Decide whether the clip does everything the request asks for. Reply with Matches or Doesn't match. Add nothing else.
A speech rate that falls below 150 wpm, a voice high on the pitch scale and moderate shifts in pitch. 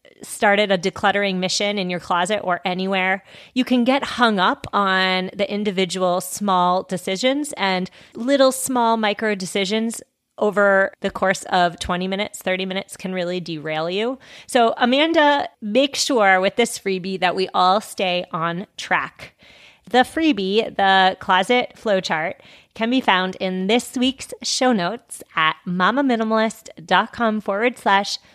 Matches